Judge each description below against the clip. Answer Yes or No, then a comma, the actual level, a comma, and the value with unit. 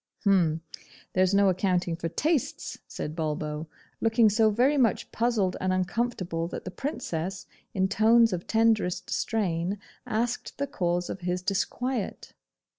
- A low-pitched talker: No, high, 190 Hz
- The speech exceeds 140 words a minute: No, slow, 135 wpm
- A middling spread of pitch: Yes, average, 4.4 semitones